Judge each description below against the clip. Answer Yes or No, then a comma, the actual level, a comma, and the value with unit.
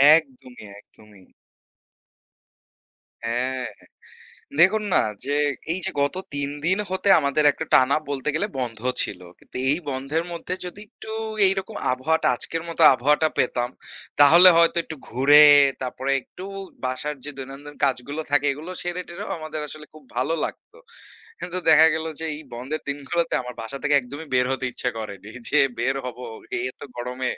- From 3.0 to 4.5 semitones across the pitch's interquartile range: Yes, average, 4.0 semitones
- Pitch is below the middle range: No, medium, 145 Hz